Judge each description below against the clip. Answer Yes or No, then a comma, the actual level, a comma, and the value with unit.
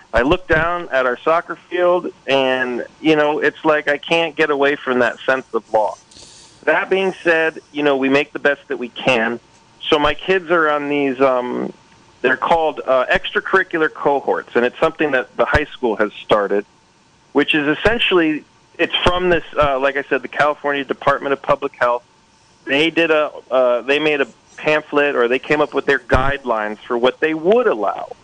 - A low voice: No, medium, 145 Hz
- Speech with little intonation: No, average, 3.4 semitones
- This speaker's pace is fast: No, average, 185 wpm